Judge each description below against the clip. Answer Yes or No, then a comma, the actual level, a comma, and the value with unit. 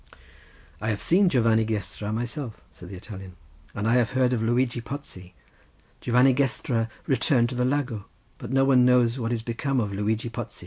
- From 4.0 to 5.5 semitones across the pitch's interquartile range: No, average, 2.7 semitones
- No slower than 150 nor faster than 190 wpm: Yes, average, 175 wpm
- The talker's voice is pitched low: Yes, low, 120 Hz